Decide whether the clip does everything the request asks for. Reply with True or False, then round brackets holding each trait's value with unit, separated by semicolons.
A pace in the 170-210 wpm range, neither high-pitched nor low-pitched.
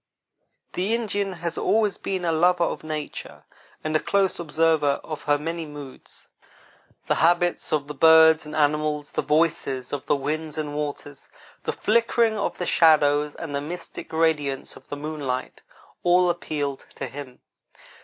False (155 wpm; 155 Hz)